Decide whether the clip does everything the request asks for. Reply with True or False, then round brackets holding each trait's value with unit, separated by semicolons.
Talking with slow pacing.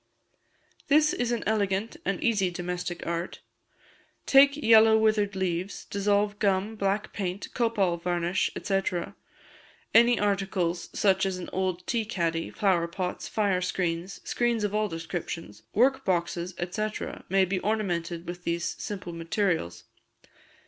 True (130 wpm)